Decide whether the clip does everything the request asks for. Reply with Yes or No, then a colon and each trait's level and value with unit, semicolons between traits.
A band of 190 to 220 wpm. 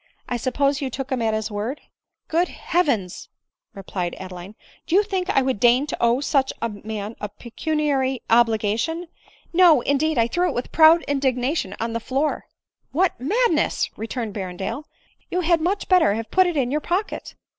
Yes: average, 200 wpm